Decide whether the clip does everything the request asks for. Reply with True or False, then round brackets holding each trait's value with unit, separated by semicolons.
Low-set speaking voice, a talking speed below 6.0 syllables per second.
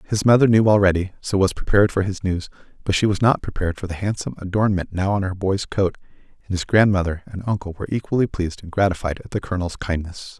False (95 Hz; 6.7 syllables/s)